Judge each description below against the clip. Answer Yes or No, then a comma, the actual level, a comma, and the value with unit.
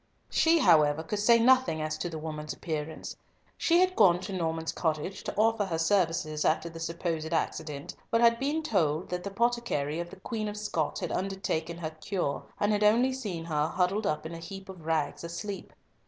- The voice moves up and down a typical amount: Yes, average, 4.8 semitones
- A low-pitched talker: No, medium, 175 Hz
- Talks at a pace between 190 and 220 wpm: Yes, average, 200 wpm